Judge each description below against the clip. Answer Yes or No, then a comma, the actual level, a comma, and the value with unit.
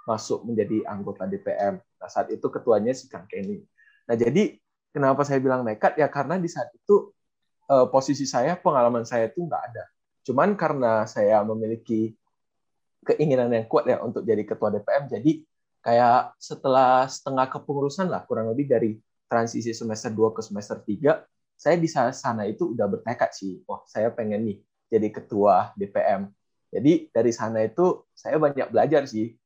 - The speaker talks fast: Yes, fast, 160 wpm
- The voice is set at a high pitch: No, low, 135 Hz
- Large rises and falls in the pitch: Yes, wide, 7.3 semitones